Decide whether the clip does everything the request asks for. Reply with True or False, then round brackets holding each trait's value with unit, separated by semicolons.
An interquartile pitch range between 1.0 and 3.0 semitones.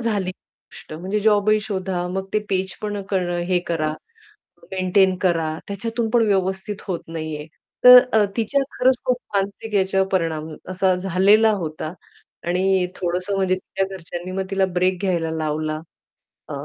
True (2.5 semitones)